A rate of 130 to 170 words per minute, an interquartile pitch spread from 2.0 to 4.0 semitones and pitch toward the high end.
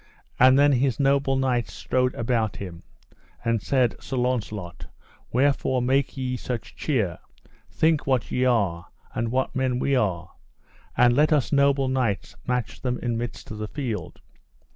No: average, 155 wpm; average, 2.7 semitones; low, 125 Hz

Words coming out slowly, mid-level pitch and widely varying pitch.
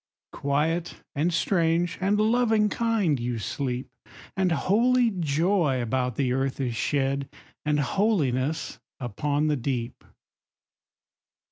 Yes: slow, 110 wpm; medium, 150 Hz; wide, 6.4 semitones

